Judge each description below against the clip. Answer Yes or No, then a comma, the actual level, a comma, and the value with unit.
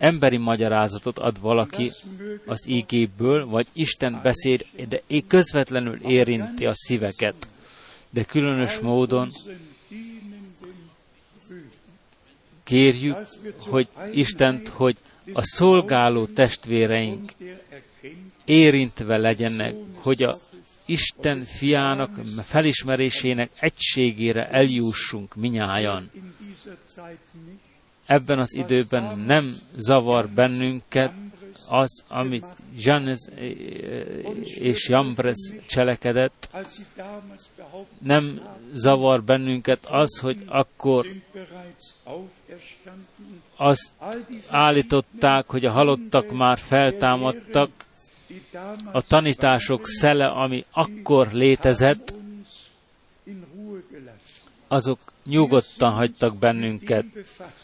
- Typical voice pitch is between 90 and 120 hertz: No, low, 135 Hz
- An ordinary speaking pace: No, slow, 70 wpm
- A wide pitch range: Yes, wide, 5.7 semitones